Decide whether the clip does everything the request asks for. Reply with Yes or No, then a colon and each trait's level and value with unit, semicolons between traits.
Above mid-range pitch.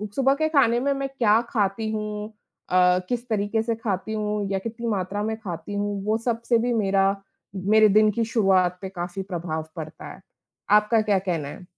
Yes: high, 210 Hz